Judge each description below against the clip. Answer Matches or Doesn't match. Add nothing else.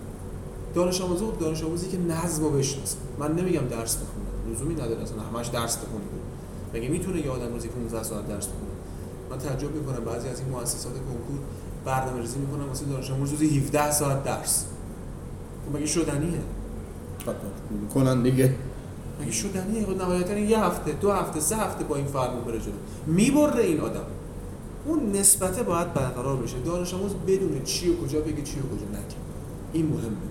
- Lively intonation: Matches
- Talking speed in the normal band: Doesn't match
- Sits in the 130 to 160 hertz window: Matches